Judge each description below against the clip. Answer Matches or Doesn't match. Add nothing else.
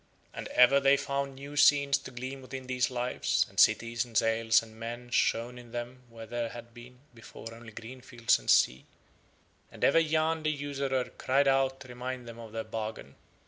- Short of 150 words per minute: Doesn't match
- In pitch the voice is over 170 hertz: Doesn't match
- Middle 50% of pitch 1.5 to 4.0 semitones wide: Matches